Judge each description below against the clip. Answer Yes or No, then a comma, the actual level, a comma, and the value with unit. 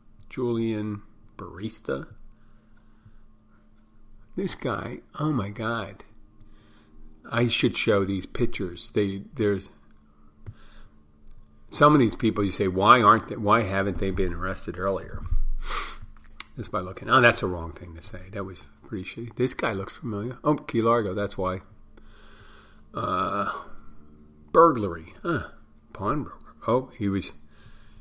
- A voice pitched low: Yes, low, 105 Hz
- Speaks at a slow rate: Yes, slow, 125 wpm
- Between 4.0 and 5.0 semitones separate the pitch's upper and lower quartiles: No, average, 3.4 semitones